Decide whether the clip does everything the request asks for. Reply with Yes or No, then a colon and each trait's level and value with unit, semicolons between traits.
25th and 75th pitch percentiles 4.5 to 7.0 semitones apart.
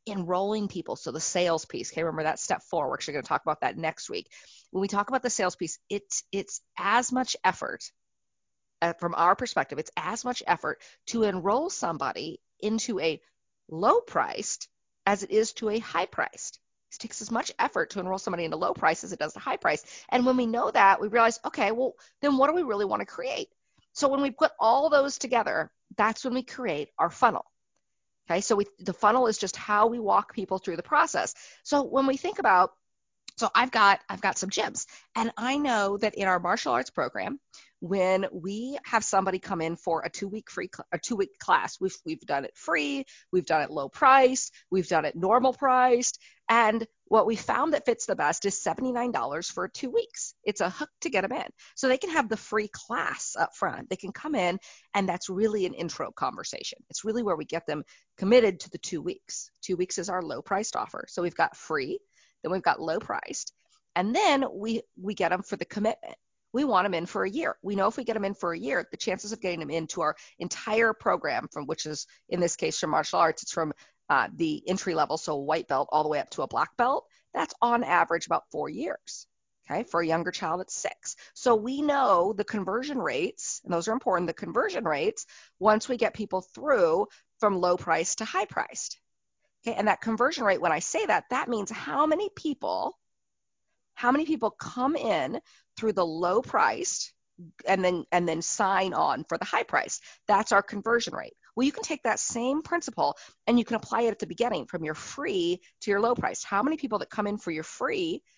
Yes: wide, 5.6 semitones